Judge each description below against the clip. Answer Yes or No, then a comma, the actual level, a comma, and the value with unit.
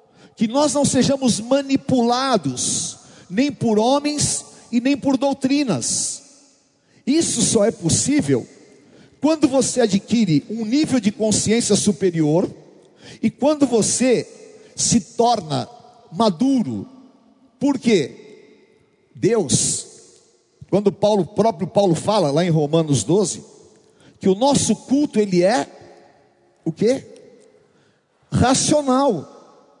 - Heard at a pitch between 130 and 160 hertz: No, high, 235 Hz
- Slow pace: Yes, slow, 100 wpm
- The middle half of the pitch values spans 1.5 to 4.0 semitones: No, average, 4.9 semitones